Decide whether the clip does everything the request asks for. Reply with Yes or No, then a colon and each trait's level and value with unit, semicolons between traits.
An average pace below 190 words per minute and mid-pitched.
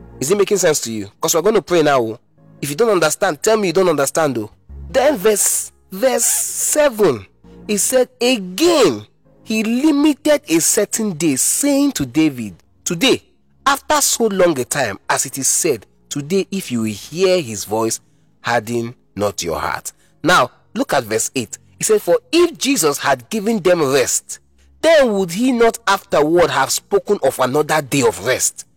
Yes: average, 175 wpm; medium, 180 Hz